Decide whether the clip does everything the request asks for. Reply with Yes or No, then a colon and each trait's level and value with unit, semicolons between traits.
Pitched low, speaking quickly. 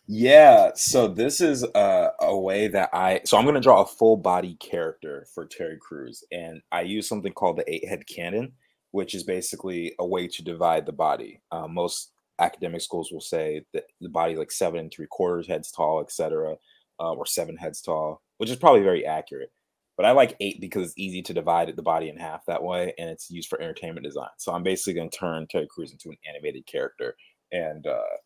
No: very high, 340 Hz; fast, 220 wpm